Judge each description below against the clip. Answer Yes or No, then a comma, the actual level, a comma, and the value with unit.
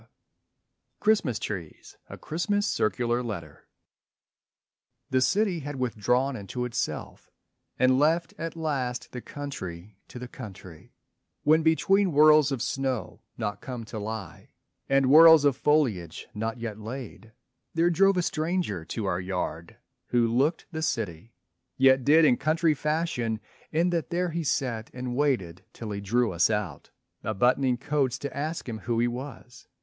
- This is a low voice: Yes, low, 130 Hz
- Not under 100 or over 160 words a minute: Yes, average, 150 wpm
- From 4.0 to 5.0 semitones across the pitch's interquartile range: No, wide, 5.6 semitones